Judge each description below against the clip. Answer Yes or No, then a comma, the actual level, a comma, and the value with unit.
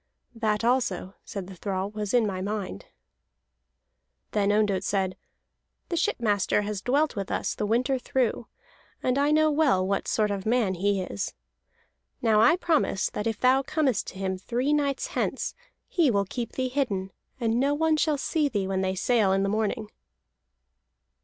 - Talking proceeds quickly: No, average, 170 wpm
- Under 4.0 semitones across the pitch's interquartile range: No, average, 5.1 semitones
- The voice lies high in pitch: Yes, high, 215 Hz